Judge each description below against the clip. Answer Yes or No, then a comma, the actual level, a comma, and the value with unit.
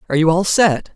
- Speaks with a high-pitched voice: No, medium, 175 Hz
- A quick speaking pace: Yes, fast, 250 wpm